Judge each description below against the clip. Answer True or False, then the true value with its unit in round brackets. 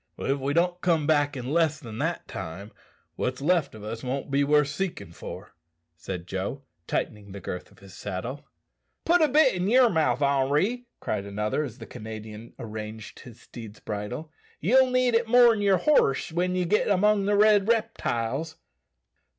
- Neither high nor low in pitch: True (145 Hz)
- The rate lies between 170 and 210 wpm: True (180 wpm)